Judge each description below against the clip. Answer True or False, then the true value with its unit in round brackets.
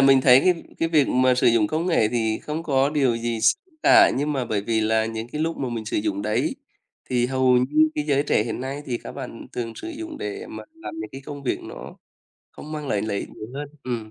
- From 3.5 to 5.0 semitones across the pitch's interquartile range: True (4.7 semitones)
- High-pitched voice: False (130 Hz)